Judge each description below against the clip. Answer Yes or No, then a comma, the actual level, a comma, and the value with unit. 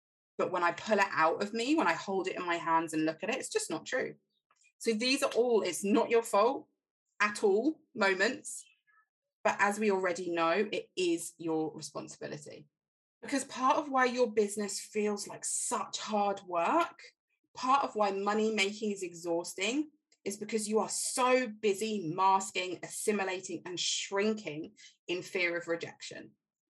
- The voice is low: No, high, 210 Hz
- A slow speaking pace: No, average, 170 wpm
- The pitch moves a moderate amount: No, wide, 5.9 semitones